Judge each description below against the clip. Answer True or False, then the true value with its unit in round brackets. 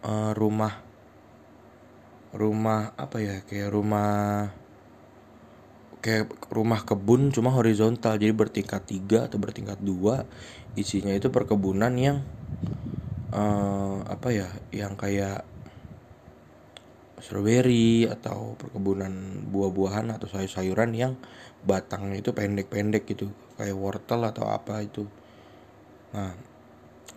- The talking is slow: False (95 wpm)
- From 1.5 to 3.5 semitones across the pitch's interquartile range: True (2.4 semitones)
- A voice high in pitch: False (105 Hz)